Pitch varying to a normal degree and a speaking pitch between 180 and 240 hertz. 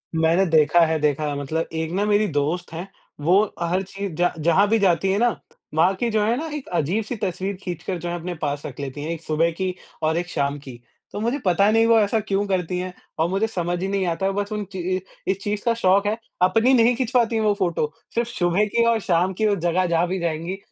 Yes: average, 3.9 semitones; medium, 185 Hz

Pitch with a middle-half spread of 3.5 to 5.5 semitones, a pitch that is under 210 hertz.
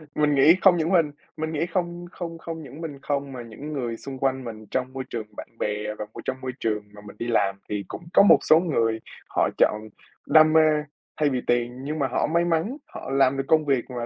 Yes: average, 4.9 semitones; low, 135 Hz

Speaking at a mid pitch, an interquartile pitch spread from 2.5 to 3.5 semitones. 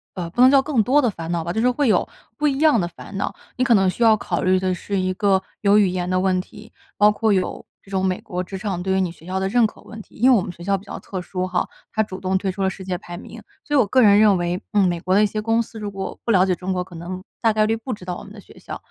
No: high, 195 Hz; average, 3.0 semitones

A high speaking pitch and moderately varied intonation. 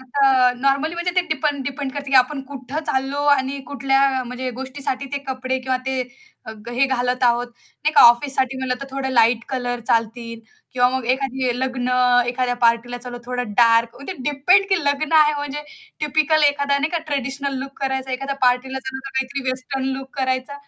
No: very high, 265 Hz; narrow, 2.0 semitones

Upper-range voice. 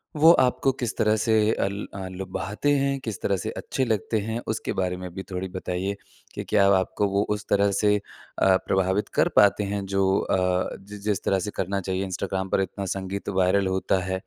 No: low, 100 Hz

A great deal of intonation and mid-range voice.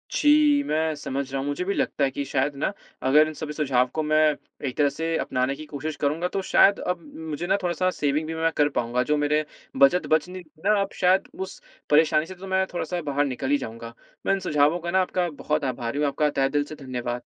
No: average, 3.8 semitones; medium, 150 Hz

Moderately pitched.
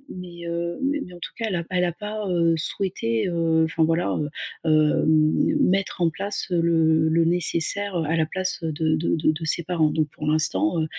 Yes: medium, 170 Hz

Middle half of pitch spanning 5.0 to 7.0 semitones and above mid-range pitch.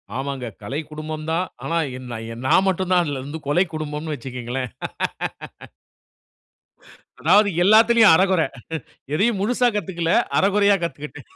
No: wide, 5.5 semitones; medium, 165 Hz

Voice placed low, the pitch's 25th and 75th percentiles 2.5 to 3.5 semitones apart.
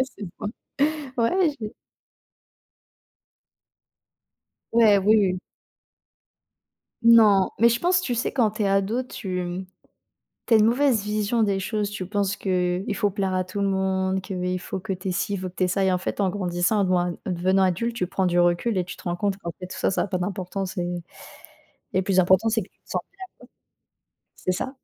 No: high, 195 Hz; average, 2.8 semitones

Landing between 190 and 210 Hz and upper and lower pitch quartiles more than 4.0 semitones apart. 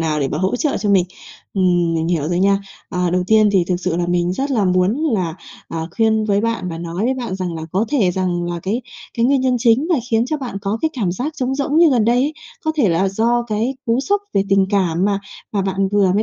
Yes: high, 200 Hz; average, 5.0 semitones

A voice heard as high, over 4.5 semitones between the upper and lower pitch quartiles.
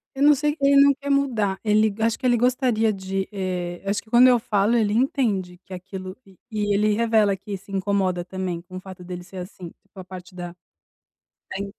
No: high, 200 Hz; average, 3.7 semitones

